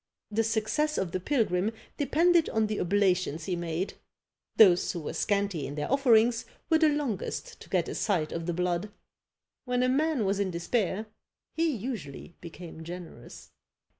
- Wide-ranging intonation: Yes, wide, 6.1 semitones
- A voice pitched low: No, high, 205 Hz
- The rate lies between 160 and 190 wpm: Yes, average, 165 wpm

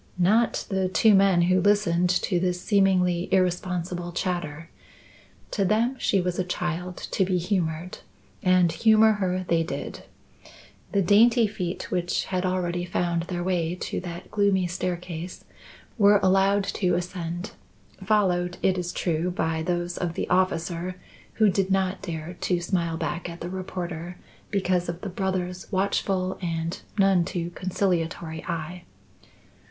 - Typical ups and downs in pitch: No, narrow, 1.7 semitones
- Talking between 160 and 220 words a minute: No, average, 145 wpm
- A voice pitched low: No, medium, 180 Hz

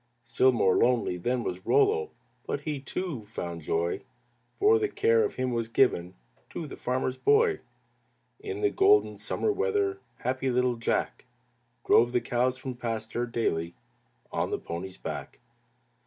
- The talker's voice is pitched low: Yes, low, 125 Hz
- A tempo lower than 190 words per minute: Yes, average, 150 wpm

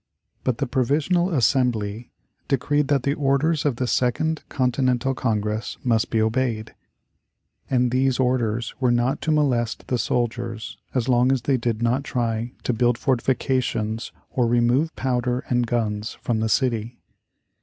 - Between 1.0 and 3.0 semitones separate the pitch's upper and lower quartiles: Yes, narrow, 2.4 semitones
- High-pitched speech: No, low, 125 Hz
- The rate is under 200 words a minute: Yes, average, 145 wpm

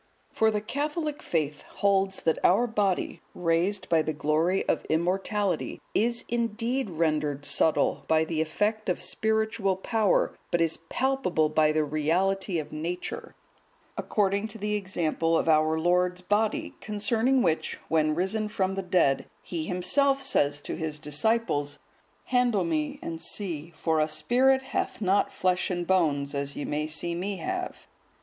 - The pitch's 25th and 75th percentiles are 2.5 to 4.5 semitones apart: No, wide, 5.4 semitones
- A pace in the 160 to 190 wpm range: No, average, 150 wpm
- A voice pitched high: No, medium, 180 Hz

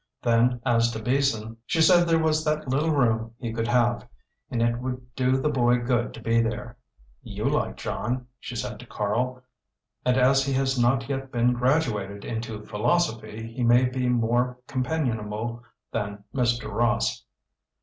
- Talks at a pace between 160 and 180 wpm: Yes, average, 165 wpm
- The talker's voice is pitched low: Yes, low, 120 Hz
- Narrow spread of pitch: Yes, narrow, 2.3 semitones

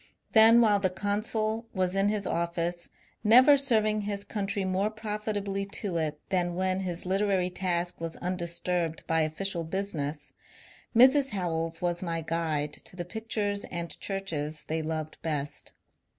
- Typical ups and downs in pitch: Yes, average, 3.7 semitones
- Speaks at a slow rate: No, average, 150 wpm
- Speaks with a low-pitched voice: No, medium, 185 Hz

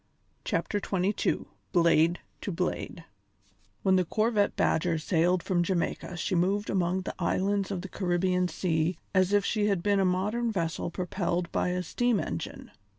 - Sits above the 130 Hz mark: Yes, medium, 185 Hz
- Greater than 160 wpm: No, average, 155 wpm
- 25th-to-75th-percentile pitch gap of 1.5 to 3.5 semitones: Yes, narrow, 2.5 semitones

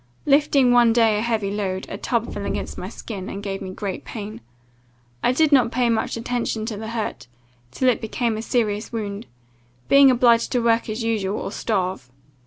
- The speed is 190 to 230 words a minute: Yes, average, 195 wpm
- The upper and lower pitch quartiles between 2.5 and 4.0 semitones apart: Yes, average, 2.9 semitones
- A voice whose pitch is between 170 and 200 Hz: No, high, 225 Hz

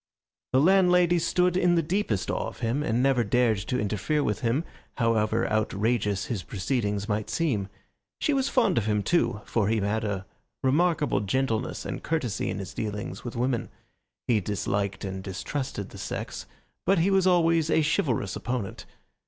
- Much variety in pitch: Yes, wide, 7.4 semitones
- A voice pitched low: Yes, low, 120 Hz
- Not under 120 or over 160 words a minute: No, average, 170 wpm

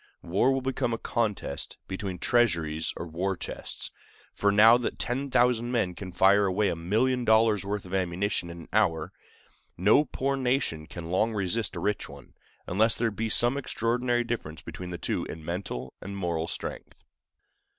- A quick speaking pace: No, average, 170 wpm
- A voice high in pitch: No, low, 100 Hz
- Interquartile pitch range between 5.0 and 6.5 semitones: Yes, average, 5.3 semitones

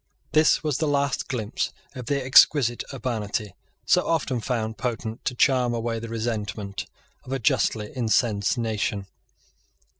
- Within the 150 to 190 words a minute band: No, average, 140 wpm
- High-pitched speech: No, low, 120 Hz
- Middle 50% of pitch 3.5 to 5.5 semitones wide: No, average, 3.0 semitones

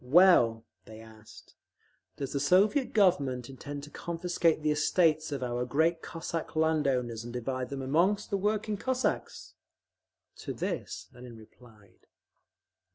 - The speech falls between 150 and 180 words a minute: No, slow, 135 wpm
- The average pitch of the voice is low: No, medium, 145 Hz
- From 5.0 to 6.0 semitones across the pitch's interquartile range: Yes, wide, 5.6 semitones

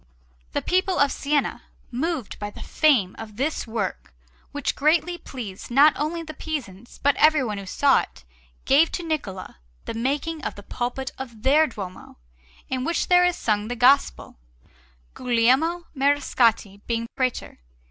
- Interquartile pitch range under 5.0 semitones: No, wide, 5.4 semitones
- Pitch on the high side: Yes, very high, 265 Hz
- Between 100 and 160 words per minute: Yes, average, 150 wpm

